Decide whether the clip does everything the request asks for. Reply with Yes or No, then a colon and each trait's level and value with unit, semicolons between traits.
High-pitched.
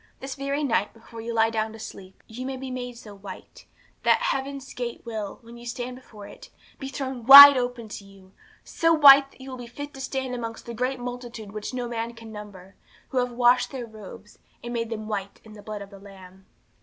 Yes: high, 235 Hz